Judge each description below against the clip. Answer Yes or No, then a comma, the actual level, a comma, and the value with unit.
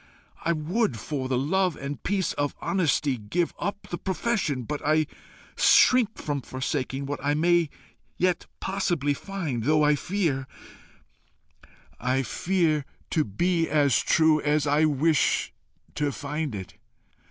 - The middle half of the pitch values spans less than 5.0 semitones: Yes, average, 3.8 semitones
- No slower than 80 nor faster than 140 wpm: Yes, slow, 135 wpm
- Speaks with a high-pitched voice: No, medium, 150 Hz